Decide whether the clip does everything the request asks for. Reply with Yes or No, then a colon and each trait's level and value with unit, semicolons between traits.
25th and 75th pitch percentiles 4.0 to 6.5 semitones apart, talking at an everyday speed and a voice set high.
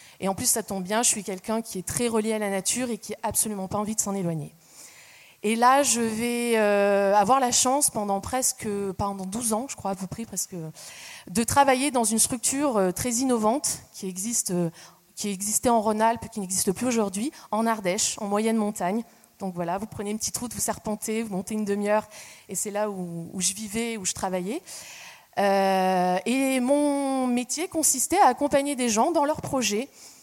No: average, 3.6 semitones; average, 200 wpm; high, 220 Hz